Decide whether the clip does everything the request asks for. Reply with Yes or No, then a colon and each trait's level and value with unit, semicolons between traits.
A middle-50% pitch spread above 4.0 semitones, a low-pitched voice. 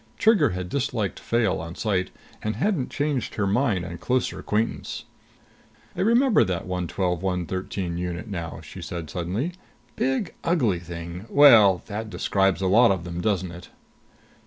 Yes: wide, 5.6 semitones; very low, 95 Hz